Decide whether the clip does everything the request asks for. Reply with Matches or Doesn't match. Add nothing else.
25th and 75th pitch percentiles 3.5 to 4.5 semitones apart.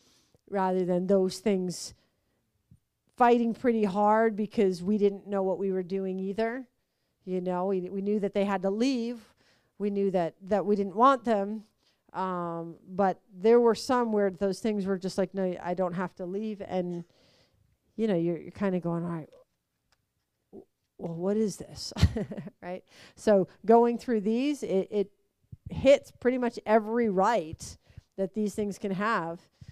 Doesn't match